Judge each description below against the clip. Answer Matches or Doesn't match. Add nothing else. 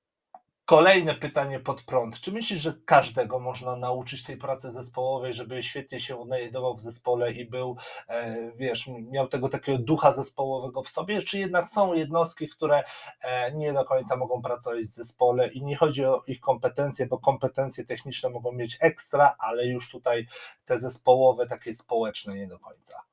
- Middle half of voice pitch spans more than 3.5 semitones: Doesn't match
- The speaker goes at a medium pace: Doesn't match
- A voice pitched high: Doesn't match